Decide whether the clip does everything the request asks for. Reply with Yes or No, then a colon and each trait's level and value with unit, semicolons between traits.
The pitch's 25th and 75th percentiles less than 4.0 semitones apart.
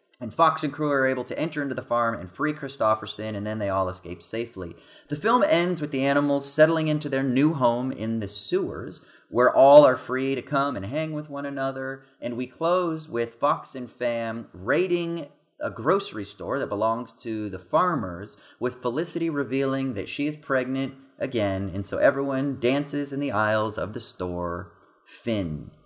No: average, 4.7 semitones